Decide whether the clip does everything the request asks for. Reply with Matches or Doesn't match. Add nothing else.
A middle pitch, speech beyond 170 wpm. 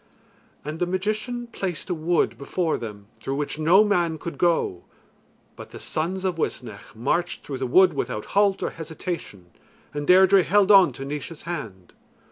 Doesn't match